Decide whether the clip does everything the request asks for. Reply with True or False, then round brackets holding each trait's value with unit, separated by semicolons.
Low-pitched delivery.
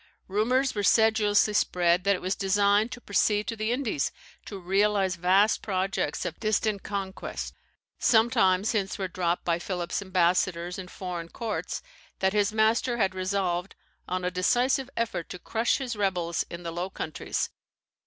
False (195 Hz)